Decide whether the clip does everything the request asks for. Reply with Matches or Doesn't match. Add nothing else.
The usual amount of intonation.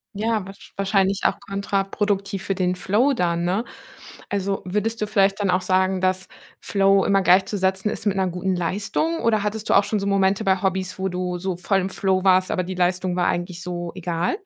Doesn't match